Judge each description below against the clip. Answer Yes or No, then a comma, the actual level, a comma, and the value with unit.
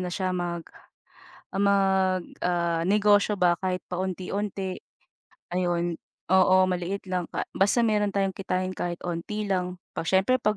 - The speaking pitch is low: No, medium, 185 Hz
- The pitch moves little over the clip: Yes, narrow, 1.9 semitones